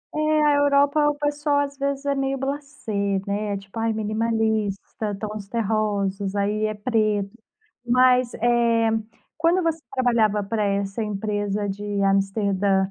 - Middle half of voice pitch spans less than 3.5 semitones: No, average, 5.1 semitones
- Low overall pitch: No, high, 220 Hz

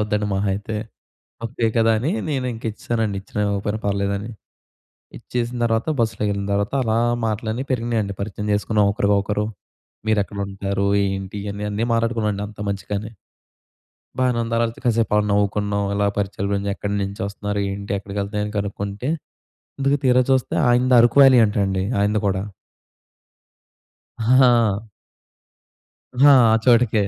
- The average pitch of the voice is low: Yes, low, 105 Hz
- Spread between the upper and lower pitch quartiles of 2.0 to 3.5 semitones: Yes, narrow, 2.4 semitones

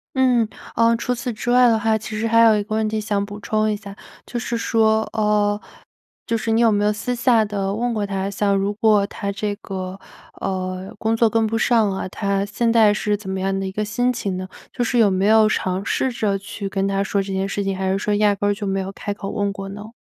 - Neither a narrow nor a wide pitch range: No, narrow, 2.2 semitones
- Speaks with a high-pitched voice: Yes, high, 210 Hz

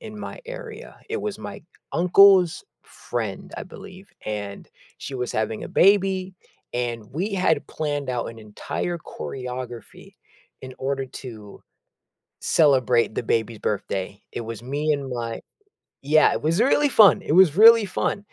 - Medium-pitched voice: Yes, medium, 145 Hz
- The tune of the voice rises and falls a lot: Yes, wide, 8.3 semitones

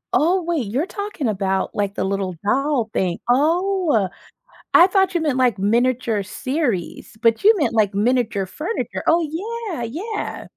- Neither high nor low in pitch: No, very high, 250 Hz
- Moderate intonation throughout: No, wide, 8.3 semitones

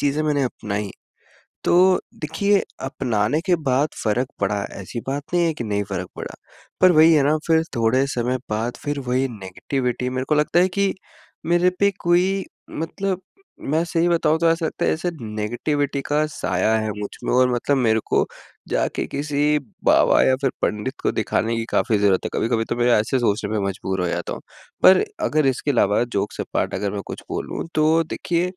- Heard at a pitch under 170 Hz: Yes, low, 135 Hz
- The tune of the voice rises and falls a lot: Yes, wide, 6.2 semitones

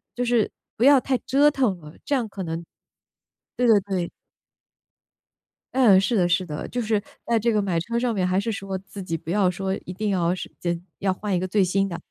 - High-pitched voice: Yes, high, 195 Hz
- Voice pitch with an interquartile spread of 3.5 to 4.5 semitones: Yes, average, 4.2 semitones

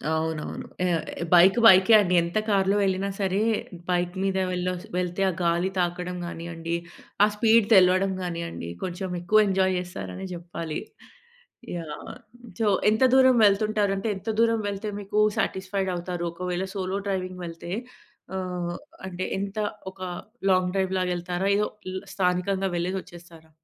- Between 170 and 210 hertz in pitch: Yes, medium, 185 Hz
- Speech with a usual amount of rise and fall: No, narrow, 1.9 semitones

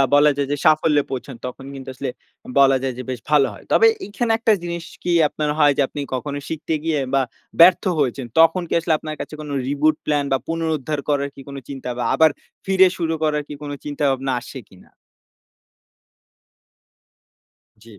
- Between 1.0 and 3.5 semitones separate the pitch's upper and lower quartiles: Yes, average, 3.0 semitones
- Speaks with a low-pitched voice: No, medium, 145 Hz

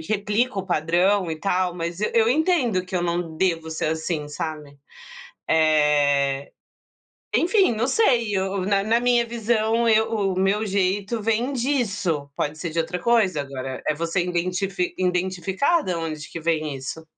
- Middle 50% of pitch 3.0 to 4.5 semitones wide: No, average, 5.3 semitones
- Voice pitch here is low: No, medium, 185 Hz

